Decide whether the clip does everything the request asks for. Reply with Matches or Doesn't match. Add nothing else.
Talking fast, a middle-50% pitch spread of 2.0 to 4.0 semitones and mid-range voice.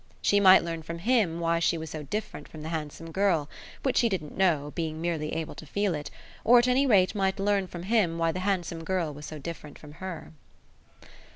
Matches